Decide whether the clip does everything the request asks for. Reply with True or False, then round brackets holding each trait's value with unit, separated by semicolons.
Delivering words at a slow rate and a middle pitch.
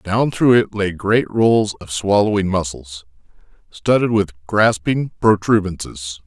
False (125 wpm; 100 Hz)